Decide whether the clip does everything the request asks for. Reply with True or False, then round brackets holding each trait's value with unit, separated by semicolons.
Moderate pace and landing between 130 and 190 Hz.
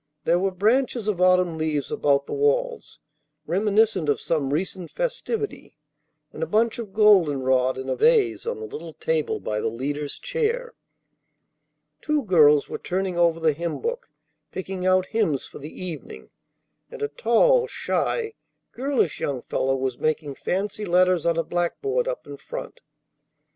True (160 wpm; 185 Hz)